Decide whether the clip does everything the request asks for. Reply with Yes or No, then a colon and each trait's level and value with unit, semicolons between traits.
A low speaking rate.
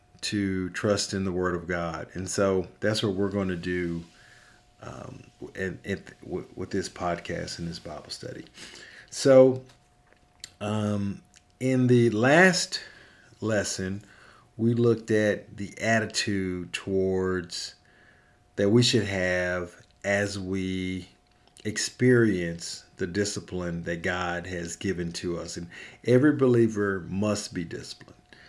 Yes: slow, 125 wpm